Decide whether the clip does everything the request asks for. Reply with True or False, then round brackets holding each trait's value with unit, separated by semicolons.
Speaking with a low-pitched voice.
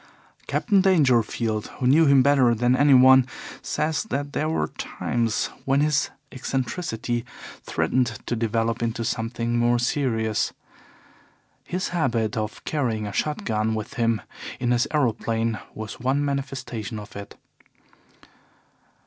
True (120 Hz)